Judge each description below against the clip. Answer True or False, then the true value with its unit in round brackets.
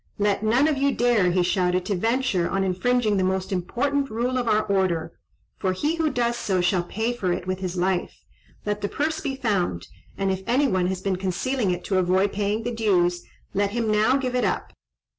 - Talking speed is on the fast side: True (215 wpm)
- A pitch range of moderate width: True (4.7 semitones)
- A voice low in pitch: False (205 Hz)